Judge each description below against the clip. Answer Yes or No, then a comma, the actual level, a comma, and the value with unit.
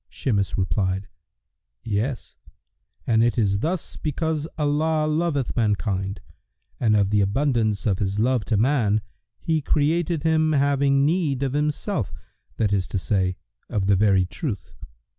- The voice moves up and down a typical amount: No, wide, 6.7 semitones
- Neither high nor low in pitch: No, low, 120 Hz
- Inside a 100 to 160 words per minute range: Yes, average, 140 wpm